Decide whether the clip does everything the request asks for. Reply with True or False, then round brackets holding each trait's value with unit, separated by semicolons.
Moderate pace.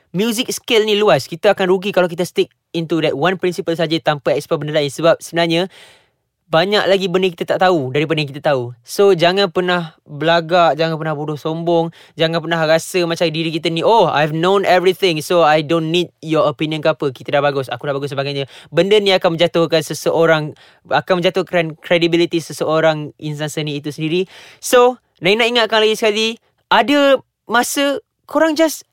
False (180 wpm)